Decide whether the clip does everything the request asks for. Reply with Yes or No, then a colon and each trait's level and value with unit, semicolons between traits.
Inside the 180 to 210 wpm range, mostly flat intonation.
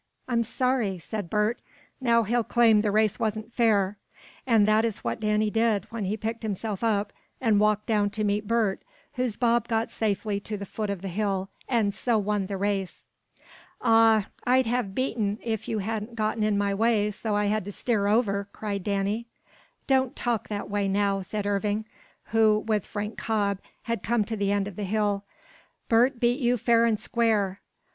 Yes: average, 185 wpm; narrow, 2.2 semitones